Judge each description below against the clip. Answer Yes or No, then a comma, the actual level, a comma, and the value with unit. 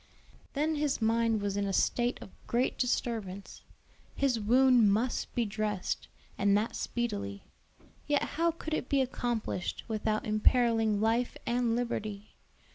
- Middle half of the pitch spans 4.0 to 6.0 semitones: No, average, 3.0 semitones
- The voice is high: Yes, high, 230 Hz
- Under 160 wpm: Yes, slow, 135 wpm